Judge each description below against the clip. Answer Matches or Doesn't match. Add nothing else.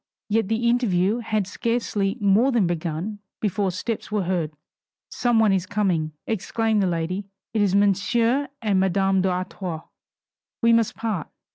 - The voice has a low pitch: Doesn't match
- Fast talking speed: Doesn't match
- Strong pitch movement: Doesn't match